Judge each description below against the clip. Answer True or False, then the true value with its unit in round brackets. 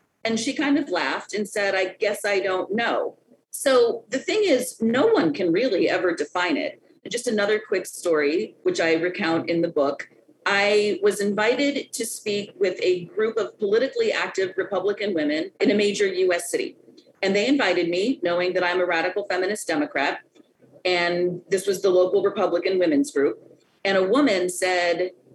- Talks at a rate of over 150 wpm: True (175 wpm)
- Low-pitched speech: False (200 Hz)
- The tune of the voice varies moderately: False (6.1 semitones)